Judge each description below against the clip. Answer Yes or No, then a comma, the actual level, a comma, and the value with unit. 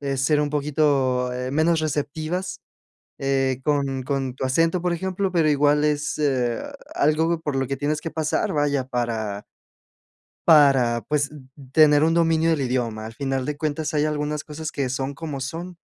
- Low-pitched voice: No, medium, 145 Hz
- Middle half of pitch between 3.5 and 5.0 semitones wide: No, average, 2.8 semitones